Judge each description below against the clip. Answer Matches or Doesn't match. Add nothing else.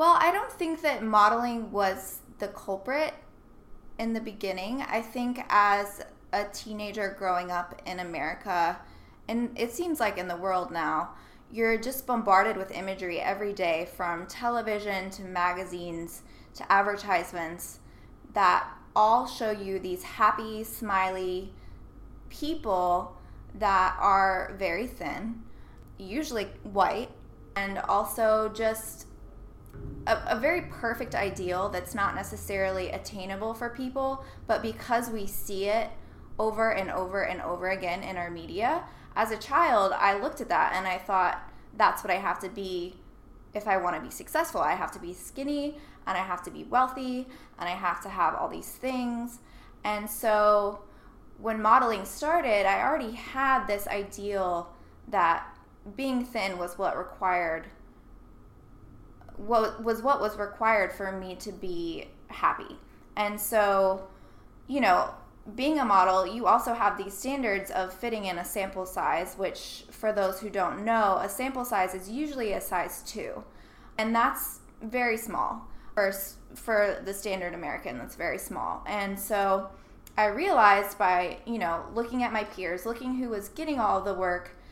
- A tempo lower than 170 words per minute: Matches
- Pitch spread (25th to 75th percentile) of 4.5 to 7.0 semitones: Doesn't match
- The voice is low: Doesn't match